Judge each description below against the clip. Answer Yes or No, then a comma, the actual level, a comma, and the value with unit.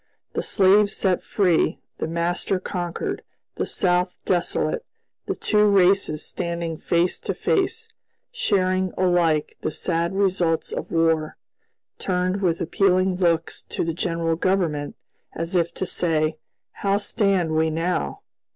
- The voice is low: No, medium, 180 Hz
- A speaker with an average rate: No, slow, 130 wpm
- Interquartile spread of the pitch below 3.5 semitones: Yes, narrow, 2.4 semitones